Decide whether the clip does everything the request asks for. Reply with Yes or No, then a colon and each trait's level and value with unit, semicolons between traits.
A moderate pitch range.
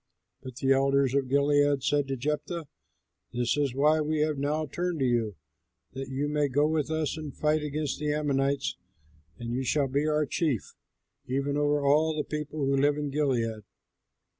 No: narrow, 2.0 semitones